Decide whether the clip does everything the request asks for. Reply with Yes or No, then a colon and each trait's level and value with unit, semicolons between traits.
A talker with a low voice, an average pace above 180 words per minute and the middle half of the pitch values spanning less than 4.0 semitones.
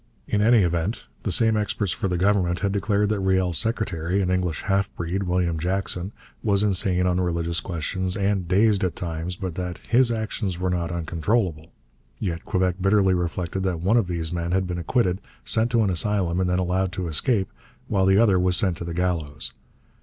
Yes: very low, 90 Hz; average, 195 wpm; narrow, 2.5 semitones